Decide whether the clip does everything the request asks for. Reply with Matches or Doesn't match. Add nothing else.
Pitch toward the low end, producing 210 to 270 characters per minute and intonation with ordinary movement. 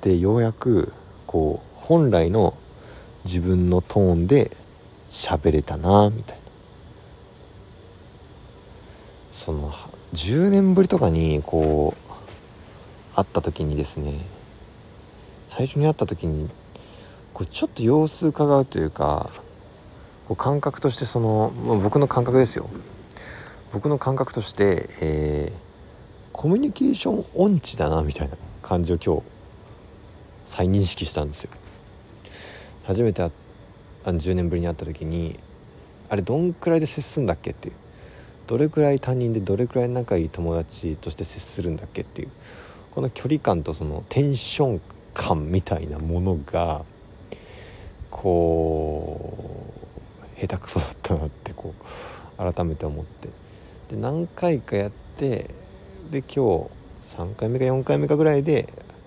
Doesn't match